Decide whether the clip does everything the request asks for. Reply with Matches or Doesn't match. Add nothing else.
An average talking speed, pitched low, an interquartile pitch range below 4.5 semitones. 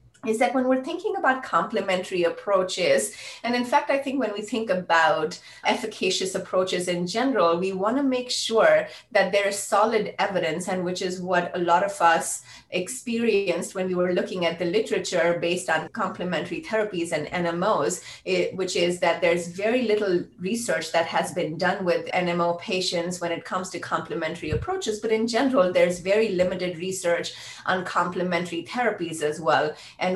Doesn't match